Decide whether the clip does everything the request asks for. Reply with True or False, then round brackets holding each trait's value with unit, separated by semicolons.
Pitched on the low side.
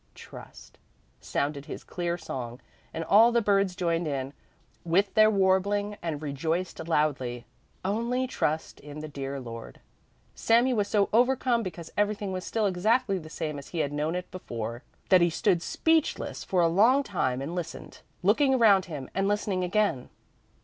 False (180 Hz)